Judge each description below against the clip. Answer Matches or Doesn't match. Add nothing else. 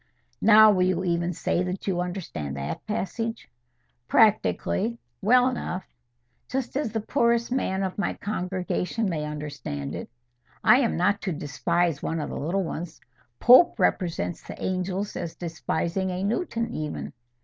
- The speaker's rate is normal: Matches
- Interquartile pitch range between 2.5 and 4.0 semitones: Doesn't match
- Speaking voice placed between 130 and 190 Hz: Matches